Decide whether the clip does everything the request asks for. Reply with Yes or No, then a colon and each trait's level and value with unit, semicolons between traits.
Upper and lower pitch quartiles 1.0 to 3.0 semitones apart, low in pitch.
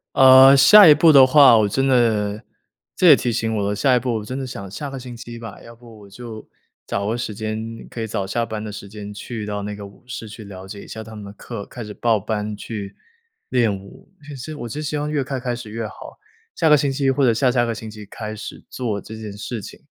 No: average, 3.7 semitones; low, 115 Hz